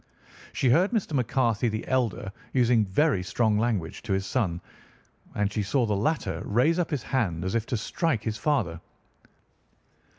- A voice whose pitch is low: Yes, low, 115 Hz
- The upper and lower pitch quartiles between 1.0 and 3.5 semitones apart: No, average, 4.7 semitones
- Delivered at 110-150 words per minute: No, average, 165 wpm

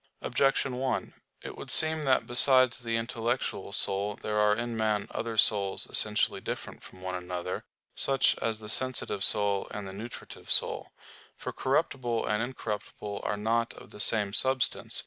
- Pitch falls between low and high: No, low, 110 Hz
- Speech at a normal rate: Yes, average, 160 wpm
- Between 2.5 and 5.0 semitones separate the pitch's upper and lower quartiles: Yes, average, 3.0 semitones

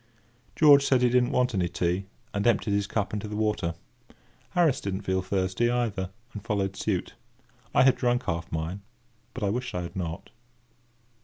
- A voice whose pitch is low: Yes, low, 100 Hz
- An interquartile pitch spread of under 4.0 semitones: No, average, 4.6 semitones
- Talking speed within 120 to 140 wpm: No, average, 180 wpm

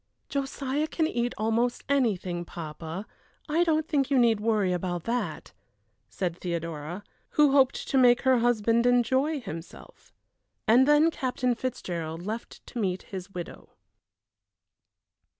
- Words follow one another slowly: Yes, slow, 130 wpm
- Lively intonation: Yes, wide, 6.6 semitones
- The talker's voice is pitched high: Yes, high, 235 Hz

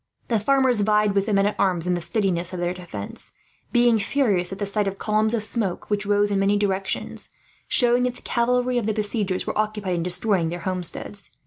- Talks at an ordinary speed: No, fast, 215 wpm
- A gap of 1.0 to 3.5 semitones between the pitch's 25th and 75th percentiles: Yes, average, 2.9 semitones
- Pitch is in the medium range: No, high, 205 Hz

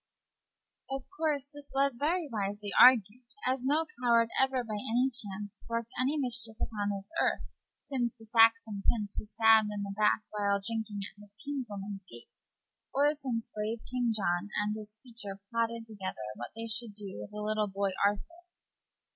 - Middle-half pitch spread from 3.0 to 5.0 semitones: Yes, average, 3.3 semitones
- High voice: Yes, high, 225 Hz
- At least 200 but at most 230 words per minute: No, average, 170 wpm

